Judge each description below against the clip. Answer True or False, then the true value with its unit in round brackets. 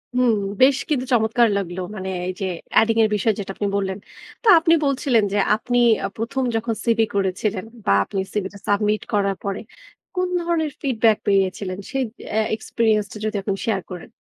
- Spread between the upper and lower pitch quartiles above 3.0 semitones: True (3.4 semitones)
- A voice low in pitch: False (220 Hz)